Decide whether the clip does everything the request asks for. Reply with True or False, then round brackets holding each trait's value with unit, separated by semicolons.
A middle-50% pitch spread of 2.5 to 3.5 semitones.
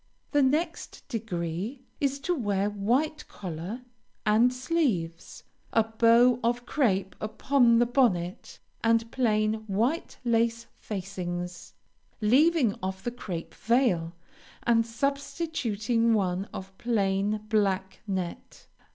False (4.3 semitones)